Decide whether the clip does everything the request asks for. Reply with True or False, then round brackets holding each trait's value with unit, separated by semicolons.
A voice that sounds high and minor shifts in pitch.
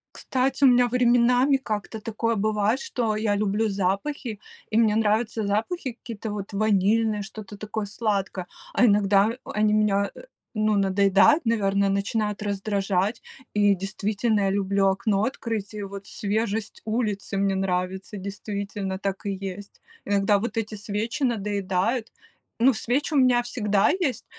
True (210 Hz; 2.3 semitones)